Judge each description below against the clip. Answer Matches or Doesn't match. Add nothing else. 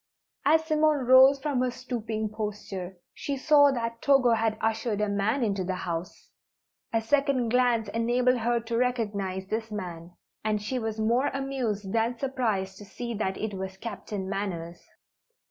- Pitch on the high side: Matches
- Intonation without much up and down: Doesn't match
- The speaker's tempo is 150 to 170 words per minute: Matches